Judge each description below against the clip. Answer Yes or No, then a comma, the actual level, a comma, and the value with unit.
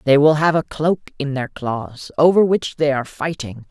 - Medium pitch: Yes, medium, 145 Hz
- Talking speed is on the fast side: Yes, fast, 210 wpm